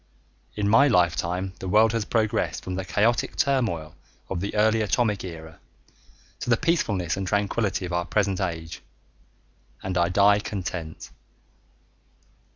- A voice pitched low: Yes, low, 100 Hz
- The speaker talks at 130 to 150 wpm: Yes, average, 140 wpm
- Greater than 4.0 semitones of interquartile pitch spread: No, average, 3.7 semitones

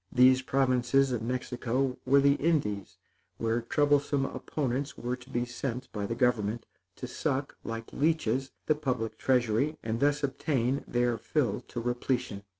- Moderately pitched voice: No, low, 125 Hz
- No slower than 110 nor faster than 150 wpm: Yes, average, 145 wpm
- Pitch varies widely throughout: No, average, 2.7 semitones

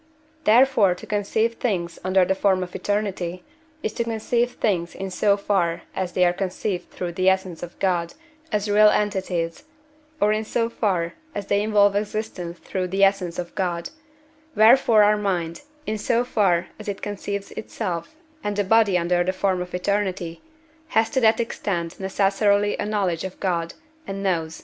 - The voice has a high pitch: Yes, high, 195 Hz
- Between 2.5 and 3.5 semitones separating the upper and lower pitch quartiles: Yes, average, 2.8 semitones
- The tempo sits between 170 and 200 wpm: Yes, average, 175 wpm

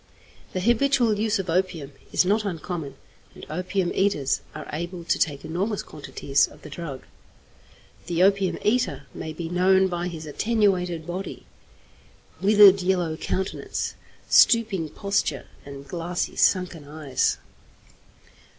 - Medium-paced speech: No, slow, 125 wpm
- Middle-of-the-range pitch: Yes, medium, 180 Hz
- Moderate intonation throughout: Yes, average, 3.8 semitones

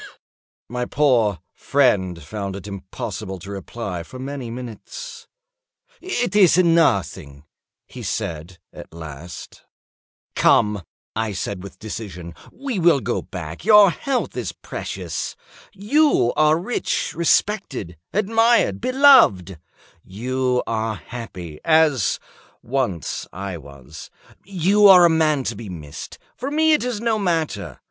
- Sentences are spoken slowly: Yes, slow, 125 wpm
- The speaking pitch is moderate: No, low, 120 Hz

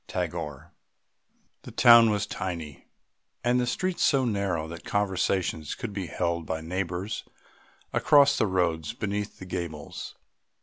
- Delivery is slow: Yes, slow, 130 wpm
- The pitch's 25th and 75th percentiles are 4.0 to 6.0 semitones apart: Yes, average, 4.5 semitones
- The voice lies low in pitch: Yes, very low, 95 Hz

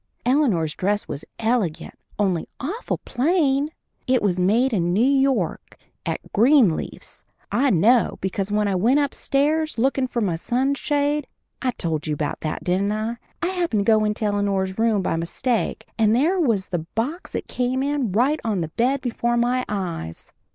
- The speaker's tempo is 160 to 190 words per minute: Yes, average, 165 wpm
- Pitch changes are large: Yes, wide, 5.9 semitones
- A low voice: No, high, 230 Hz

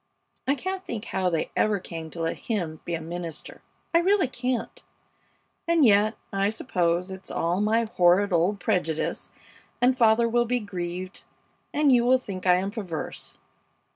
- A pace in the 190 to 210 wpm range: No, average, 165 wpm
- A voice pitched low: No, high, 200 Hz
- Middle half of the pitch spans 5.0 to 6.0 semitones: Yes, wide, 5.4 semitones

